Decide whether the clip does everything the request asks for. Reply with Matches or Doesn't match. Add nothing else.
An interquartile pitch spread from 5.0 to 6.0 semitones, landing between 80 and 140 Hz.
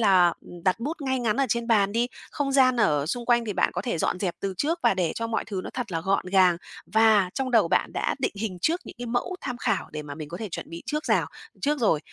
Doesn't match